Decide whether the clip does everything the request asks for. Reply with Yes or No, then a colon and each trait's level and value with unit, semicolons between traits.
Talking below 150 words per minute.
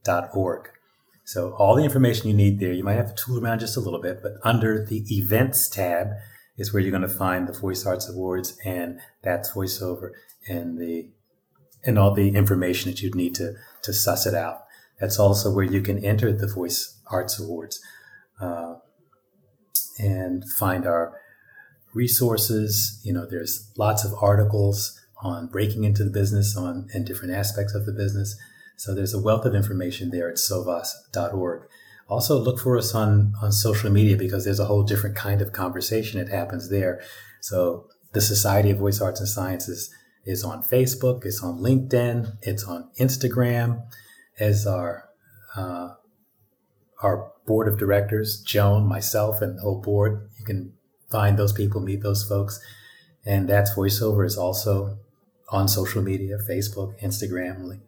No: average, 165 wpm